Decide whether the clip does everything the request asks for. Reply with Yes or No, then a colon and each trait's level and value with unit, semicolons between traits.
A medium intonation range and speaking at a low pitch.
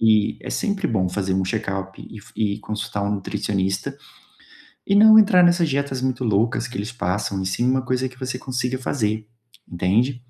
Yes: average, 4.4 semitones; low, 115 Hz